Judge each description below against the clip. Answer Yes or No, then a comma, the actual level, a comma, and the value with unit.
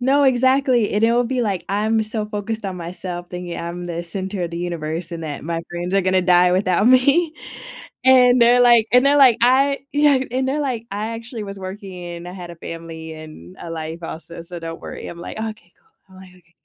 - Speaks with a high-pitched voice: Yes, high, 195 Hz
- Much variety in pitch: Yes, wide, 6.0 semitones